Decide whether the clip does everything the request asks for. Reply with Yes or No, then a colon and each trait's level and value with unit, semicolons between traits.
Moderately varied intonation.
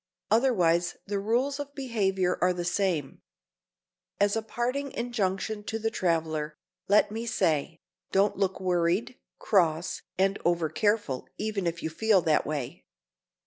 Yes: average, 4.7 semitones